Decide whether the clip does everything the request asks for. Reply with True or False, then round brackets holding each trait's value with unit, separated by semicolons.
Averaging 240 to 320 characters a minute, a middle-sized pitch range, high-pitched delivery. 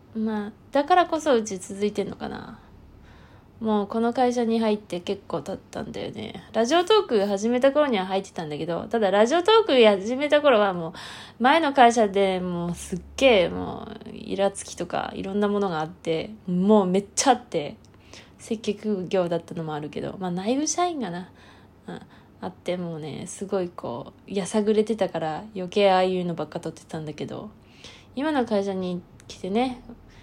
False (340 characters per minute; 4.3 semitones; 205 Hz)